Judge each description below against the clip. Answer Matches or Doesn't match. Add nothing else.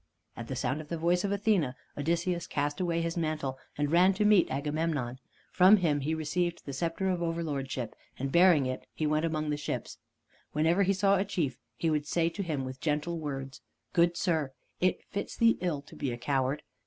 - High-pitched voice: Doesn't match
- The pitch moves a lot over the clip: Doesn't match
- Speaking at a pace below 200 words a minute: Doesn't match